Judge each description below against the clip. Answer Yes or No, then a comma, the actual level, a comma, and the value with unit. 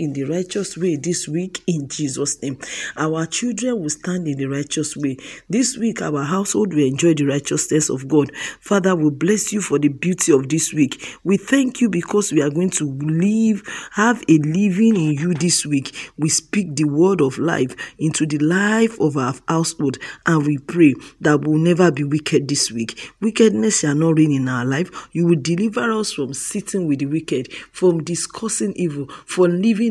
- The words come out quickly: No, average, 195 wpm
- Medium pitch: Yes, medium, 165 Hz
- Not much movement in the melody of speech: No, average, 5.1 semitones